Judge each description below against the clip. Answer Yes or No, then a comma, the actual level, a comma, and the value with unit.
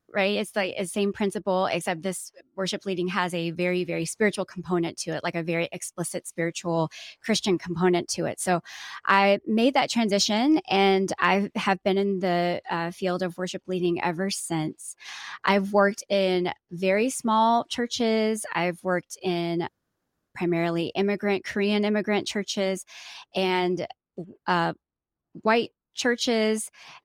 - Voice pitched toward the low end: No, high, 190 Hz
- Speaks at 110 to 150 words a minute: Yes, average, 140 wpm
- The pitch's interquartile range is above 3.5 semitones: No, average, 2.7 semitones